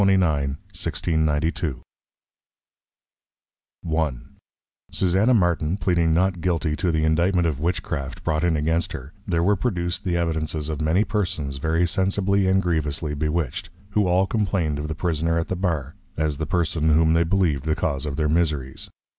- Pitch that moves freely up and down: No, average, 2.8 semitones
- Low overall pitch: Yes, very low, 80 Hz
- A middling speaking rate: Yes, average, 155 wpm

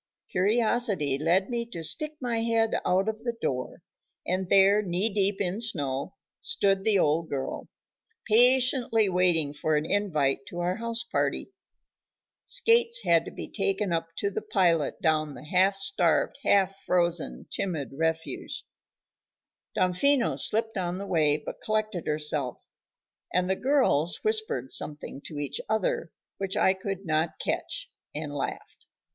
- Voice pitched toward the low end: No, high, 190 Hz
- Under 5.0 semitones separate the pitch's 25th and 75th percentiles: No, average, 5.3 semitones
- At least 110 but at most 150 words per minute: Yes, average, 140 wpm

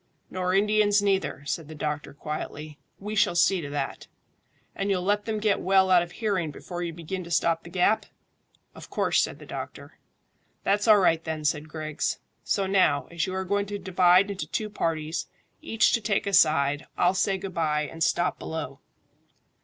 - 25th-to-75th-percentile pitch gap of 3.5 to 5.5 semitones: Yes, average, 4.1 semitones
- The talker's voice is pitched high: No, medium, 180 Hz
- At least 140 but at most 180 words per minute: No, average, 190 wpm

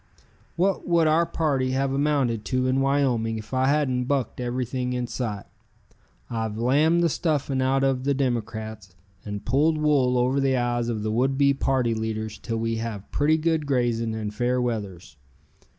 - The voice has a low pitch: Yes, low, 125 Hz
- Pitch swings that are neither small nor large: Yes, average, 3.5 semitones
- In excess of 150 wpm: Yes, average, 170 wpm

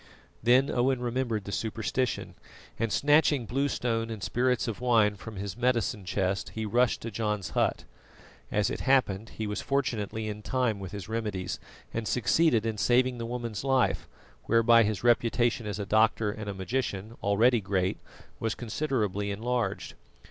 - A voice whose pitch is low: Yes, low, 115 Hz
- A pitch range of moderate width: Yes, average, 3.0 semitones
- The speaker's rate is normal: Yes, average, 160 wpm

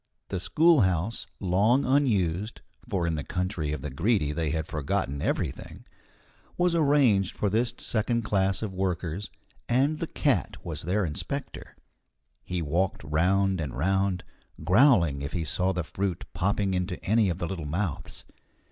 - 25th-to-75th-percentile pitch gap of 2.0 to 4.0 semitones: No, average, 4.6 semitones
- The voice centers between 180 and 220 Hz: No, very low, 95 Hz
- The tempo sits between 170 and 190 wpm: No, average, 150 wpm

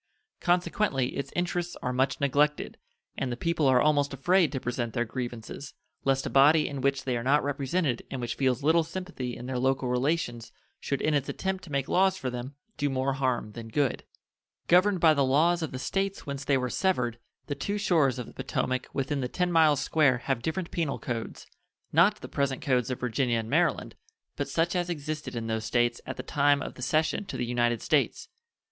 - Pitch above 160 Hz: No, medium, 140 Hz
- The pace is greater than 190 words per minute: Yes, fast, 205 wpm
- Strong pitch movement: No, average, 4.2 semitones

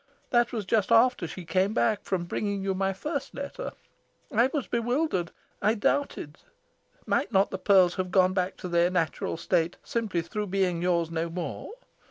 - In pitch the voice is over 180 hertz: Yes, high, 190 Hz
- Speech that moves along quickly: No, average, 175 wpm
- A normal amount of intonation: Yes, average, 4.4 semitones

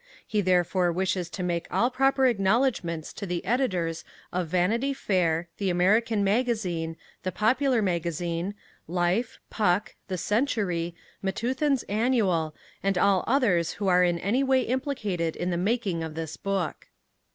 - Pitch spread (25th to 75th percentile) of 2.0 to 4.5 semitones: No, average, 5.0 semitones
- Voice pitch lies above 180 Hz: Yes, high, 190 Hz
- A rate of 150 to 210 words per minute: No, average, 140 wpm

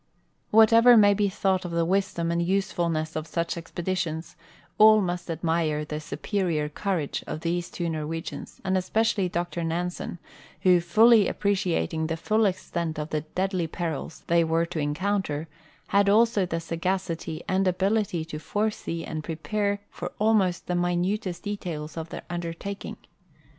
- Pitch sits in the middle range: Yes, medium, 175 Hz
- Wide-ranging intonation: No, average, 3.3 semitones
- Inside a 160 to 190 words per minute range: No, average, 150 wpm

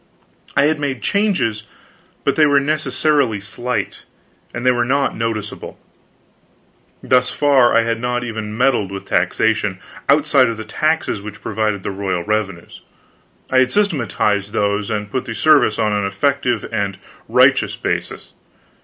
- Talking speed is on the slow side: No, average, 145 wpm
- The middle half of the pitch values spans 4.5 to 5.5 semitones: Yes, average, 4.9 semitones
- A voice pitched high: No, low, 115 Hz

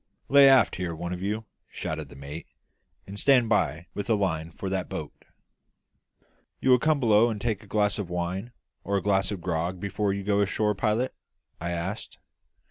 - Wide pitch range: No, average, 3.6 semitones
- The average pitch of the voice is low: Yes, low, 100 Hz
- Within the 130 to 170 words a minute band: No, average, 190 wpm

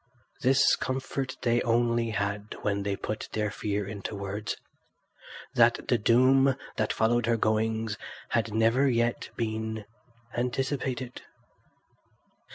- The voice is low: Yes, low, 115 Hz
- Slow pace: Yes, slow, 110 wpm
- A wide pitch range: No, narrow, 2.6 semitones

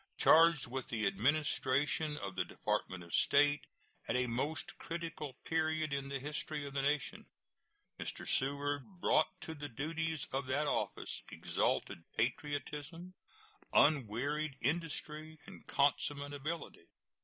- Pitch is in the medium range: Yes, medium, 145 Hz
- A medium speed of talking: No, slow, 125 wpm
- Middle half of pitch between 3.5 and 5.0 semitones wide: No, average, 2.8 semitones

